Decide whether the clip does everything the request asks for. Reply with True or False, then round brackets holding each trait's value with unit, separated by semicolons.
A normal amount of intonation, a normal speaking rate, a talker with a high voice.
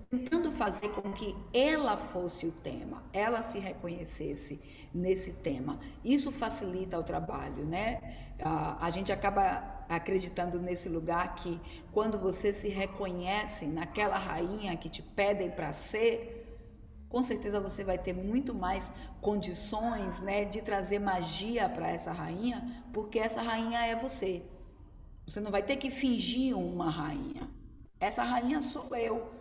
True (4.3 semitones; 140 wpm; 200 Hz)